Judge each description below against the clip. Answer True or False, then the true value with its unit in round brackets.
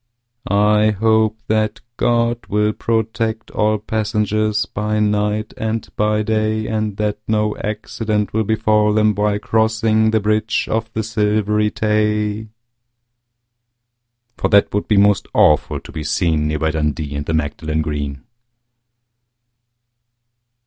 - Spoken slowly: True (130 wpm)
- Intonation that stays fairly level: True (1.1 semitones)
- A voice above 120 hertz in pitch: False (105 Hz)